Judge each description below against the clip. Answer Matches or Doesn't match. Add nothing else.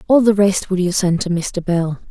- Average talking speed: Doesn't match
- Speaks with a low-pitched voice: Doesn't match